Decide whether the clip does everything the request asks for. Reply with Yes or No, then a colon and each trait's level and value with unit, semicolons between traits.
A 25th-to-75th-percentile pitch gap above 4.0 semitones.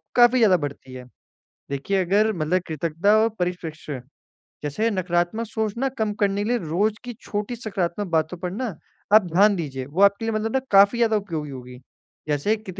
Yes: average, 5.1 semitones